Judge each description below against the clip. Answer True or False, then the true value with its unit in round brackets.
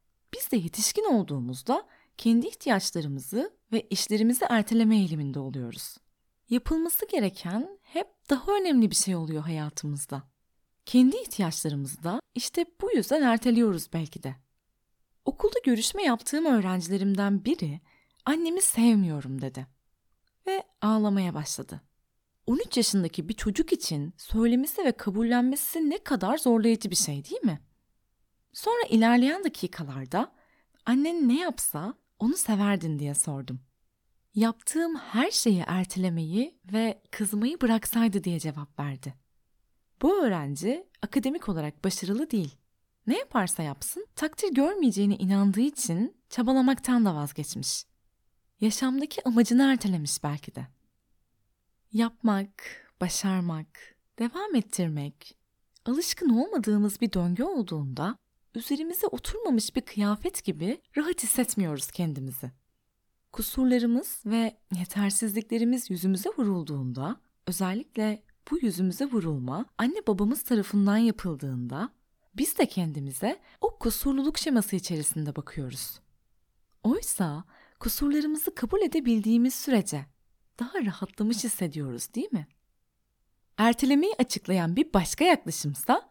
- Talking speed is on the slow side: False (105 wpm)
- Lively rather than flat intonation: True (7.8 semitones)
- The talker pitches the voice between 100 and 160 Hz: False (215 Hz)